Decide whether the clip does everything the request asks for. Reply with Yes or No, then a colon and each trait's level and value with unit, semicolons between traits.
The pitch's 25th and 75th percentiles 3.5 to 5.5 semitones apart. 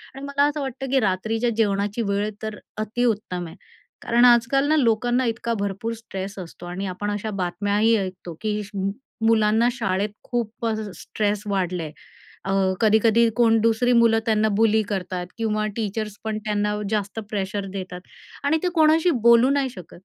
No: average, 2.8 semitones